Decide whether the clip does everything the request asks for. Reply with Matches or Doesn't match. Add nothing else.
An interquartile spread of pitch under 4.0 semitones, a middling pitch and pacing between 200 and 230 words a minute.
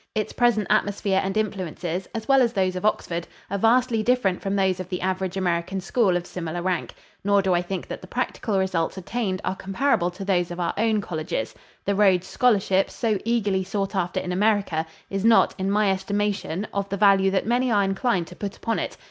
Doesn't match